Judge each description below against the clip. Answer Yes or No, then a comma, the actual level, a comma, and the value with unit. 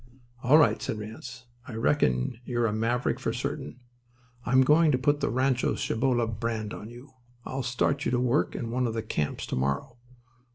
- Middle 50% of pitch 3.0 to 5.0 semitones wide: No, narrow, 2.6 semitones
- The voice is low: Yes, low, 120 Hz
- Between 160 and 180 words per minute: No, average, 190 wpm